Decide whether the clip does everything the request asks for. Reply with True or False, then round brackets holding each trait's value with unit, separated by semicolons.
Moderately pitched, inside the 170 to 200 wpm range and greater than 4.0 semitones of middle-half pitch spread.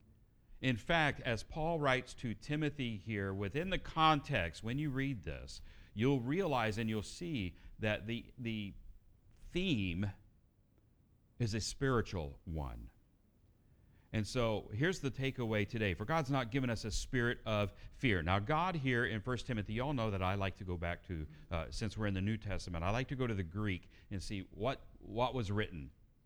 False (110 Hz; 180 wpm; 4.7 semitones)